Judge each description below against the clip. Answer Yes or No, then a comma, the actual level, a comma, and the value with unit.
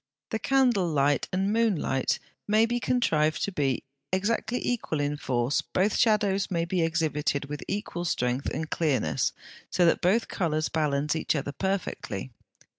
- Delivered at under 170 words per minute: Yes, average, 155 wpm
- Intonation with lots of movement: Yes, wide, 5.8 semitones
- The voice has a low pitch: No, medium, 165 Hz